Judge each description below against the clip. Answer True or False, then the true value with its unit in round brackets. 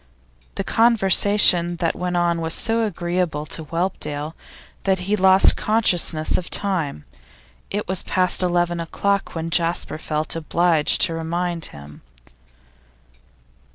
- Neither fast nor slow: False (120 wpm)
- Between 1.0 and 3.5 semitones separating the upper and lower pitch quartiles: True (2.6 semitones)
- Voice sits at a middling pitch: True (175 Hz)